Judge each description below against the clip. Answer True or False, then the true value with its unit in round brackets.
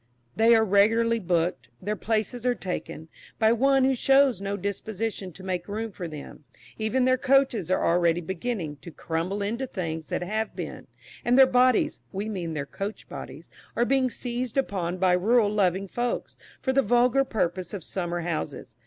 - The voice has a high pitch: True (210 Hz)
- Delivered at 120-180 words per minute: True (175 wpm)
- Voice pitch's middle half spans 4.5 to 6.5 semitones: True (5.1 semitones)